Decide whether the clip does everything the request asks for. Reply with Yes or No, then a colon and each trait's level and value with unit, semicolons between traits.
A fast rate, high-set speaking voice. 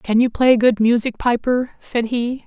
No: average, 195 wpm; high, 235 Hz